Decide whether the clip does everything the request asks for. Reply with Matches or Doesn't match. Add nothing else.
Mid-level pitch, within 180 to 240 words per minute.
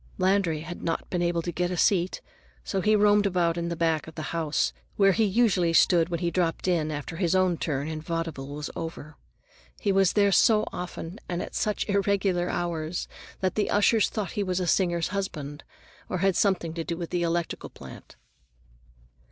Matches